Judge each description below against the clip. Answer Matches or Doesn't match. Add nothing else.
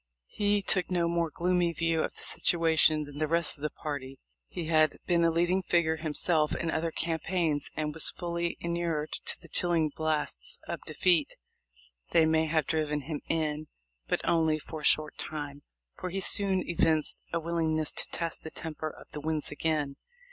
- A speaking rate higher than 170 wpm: Matches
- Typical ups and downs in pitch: Doesn't match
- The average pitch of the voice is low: Doesn't match